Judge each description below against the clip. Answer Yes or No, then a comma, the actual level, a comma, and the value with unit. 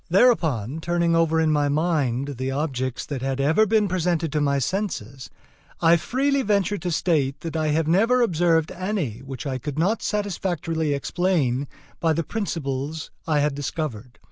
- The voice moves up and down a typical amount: Yes, average, 4.4 semitones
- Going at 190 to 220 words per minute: No, average, 165 wpm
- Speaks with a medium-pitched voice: Yes, medium, 160 Hz